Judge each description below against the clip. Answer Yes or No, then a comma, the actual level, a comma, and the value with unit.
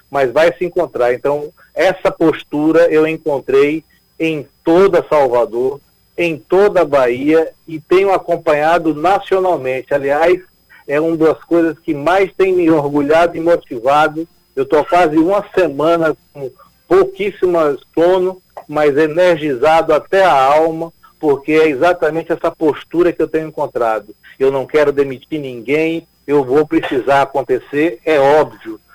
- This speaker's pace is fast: No, average, 135 wpm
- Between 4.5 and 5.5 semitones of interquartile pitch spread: No, average, 2.8 semitones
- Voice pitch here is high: No, medium, 160 Hz